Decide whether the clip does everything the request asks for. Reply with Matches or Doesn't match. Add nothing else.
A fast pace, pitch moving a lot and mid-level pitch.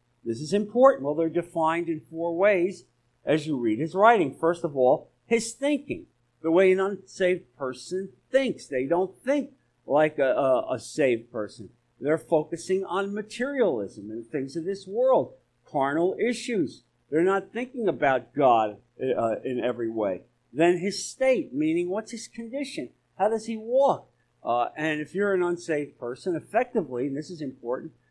Doesn't match